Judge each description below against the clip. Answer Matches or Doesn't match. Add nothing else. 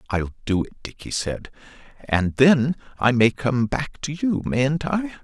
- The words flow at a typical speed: Matches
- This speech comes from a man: Matches